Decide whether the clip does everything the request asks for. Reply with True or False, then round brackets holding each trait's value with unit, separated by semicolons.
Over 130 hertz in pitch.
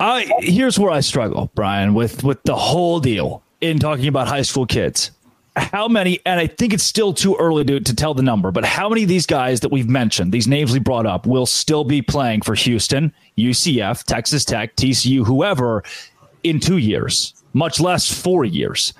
True (140 Hz)